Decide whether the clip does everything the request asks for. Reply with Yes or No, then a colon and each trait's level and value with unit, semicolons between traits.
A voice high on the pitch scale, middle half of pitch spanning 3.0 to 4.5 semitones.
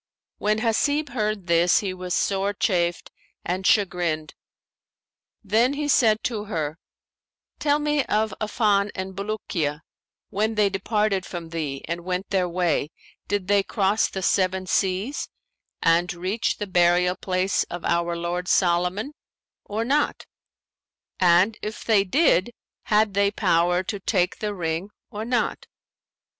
Yes: high, 195 Hz; average, 3.3 semitones